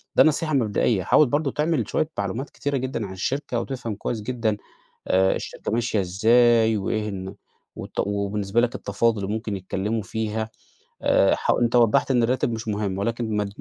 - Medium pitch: No, low, 110 Hz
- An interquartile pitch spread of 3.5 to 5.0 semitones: No, average, 3.1 semitones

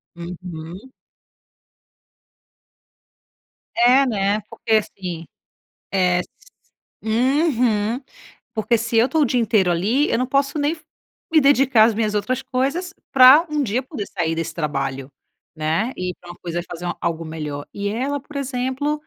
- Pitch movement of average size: No, wide, 6.9 semitones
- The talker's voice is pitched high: Yes, high, 225 Hz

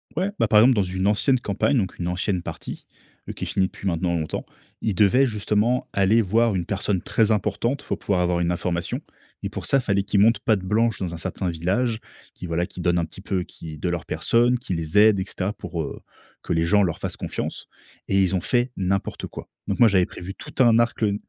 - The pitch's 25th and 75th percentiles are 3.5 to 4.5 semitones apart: Yes, average, 4.0 semitones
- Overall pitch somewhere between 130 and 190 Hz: No, low, 100 Hz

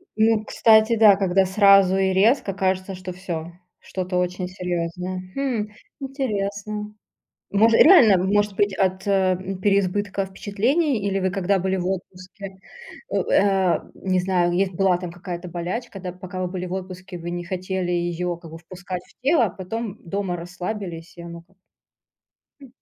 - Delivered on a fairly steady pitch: Yes, narrow, 2.1 semitones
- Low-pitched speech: No, high, 190 Hz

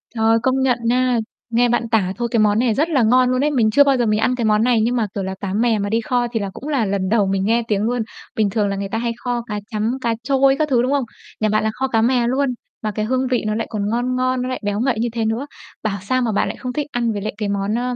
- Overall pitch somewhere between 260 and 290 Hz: No, high, 230 Hz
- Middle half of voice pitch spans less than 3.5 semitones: Yes, average, 3.0 semitones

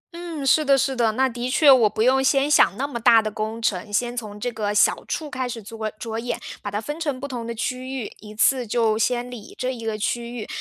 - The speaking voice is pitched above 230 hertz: Yes, high, 240 Hz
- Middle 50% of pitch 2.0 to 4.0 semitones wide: Yes, average, 3.2 semitones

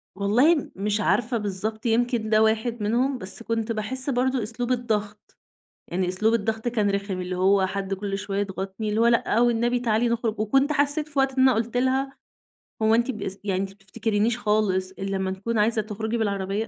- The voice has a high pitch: Yes, high, 220 Hz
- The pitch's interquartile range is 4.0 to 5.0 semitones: No, average, 3.2 semitones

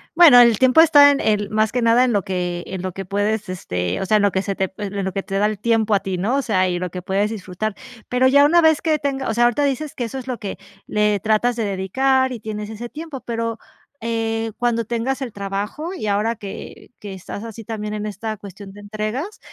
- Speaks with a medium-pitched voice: No, high, 215 Hz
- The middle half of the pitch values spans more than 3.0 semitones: Yes, average, 3.7 semitones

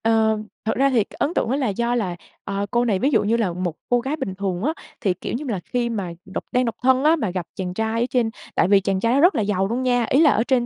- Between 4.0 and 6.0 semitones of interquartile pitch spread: Yes, average, 4.3 semitones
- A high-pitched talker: Yes, high, 225 Hz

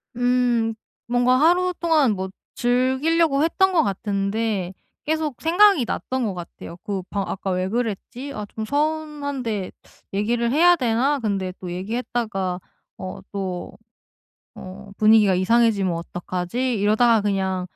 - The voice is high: Yes, high, 225 Hz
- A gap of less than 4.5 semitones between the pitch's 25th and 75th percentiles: No, wide, 5.5 semitones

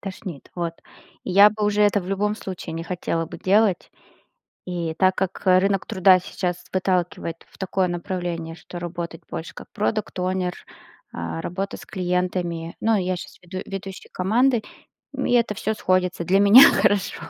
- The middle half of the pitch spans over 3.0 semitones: No, narrow, 2.4 semitones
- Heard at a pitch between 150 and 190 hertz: Yes, medium, 185 Hz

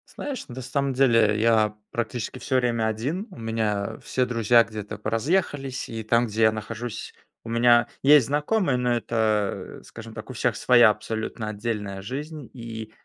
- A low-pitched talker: Yes, low, 115 Hz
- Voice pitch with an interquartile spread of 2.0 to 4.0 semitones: Yes, average, 2.8 semitones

